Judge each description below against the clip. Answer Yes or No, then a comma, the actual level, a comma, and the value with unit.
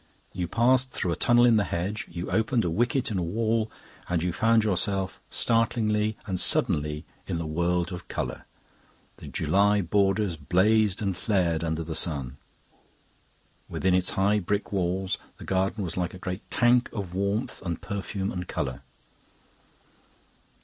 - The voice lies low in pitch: Yes, very low, 95 Hz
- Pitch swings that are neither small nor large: Yes, average, 3.6 semitones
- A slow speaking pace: No, average, 155 wpm